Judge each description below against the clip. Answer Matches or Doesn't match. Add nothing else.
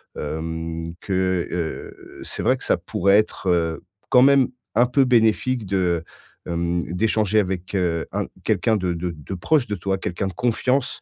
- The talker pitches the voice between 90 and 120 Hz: Matches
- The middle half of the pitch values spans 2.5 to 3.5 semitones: Doesn't match